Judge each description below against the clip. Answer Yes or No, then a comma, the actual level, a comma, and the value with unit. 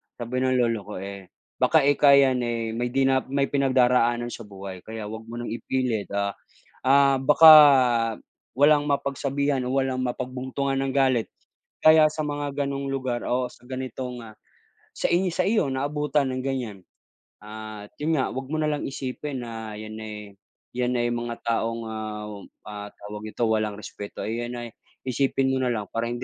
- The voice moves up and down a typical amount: Yes, average, 3.7 semitones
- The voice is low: Yes, low, 125 Hz